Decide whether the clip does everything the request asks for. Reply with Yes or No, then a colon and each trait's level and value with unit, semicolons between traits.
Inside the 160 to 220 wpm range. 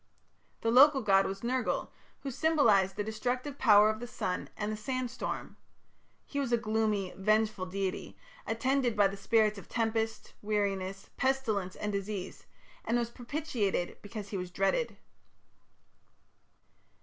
No: average, 140 wpm